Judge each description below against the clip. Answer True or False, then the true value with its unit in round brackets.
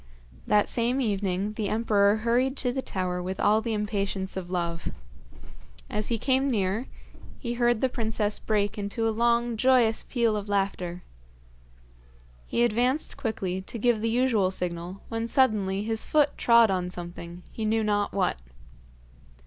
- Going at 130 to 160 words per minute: True (155 wpm)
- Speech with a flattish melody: False (3.5 semitones)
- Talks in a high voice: True (215 Hz)